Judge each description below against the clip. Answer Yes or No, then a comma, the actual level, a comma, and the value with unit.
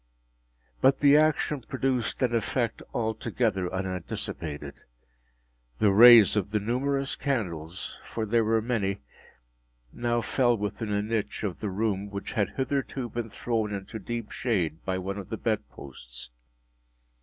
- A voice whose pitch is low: Yes, low, 110 Hz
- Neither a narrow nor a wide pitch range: Yes, average, 3.7 semitones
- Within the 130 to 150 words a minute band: Yes, average, 140 wpm